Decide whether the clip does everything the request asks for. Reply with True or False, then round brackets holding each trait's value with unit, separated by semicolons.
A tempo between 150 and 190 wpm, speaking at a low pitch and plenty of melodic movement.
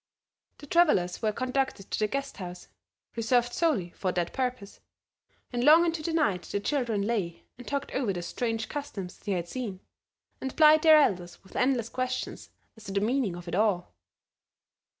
False (175 wpm; 230 Hz; 6.1 semitones)